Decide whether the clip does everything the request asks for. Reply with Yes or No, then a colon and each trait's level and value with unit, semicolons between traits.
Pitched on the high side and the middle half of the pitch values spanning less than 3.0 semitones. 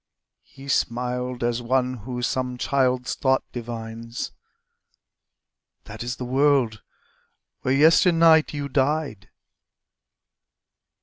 No: low, 125 Hz; narrow, 2.5 semitones